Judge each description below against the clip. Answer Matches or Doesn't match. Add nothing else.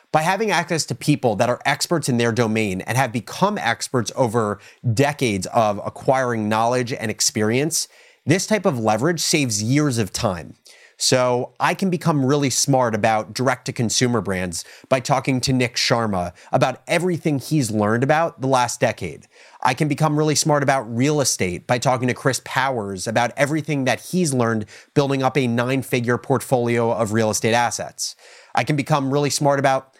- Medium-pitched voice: Doesn't match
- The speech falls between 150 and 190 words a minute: Matches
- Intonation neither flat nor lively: Matches